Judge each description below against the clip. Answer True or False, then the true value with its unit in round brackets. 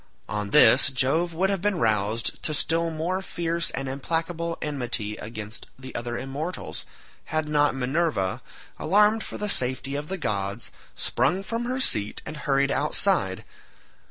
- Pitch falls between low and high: True (150 Hz)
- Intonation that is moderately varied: False (5.8 semitones)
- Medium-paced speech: True (150 wpm)